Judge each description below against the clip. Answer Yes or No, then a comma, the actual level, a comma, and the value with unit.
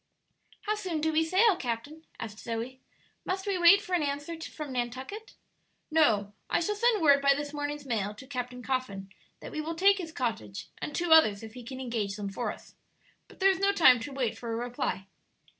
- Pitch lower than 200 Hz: No, very high, 280 Hz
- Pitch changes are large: Yes, wide, 6.3 semitones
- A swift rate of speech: Yes, fast, 210 wpm